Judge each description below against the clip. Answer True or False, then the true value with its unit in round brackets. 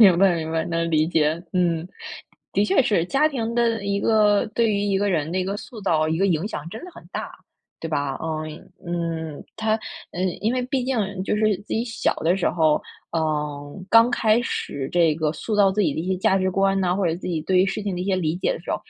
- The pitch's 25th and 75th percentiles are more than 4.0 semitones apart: True (4.5 semitones)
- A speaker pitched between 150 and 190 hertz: True (185 Hz)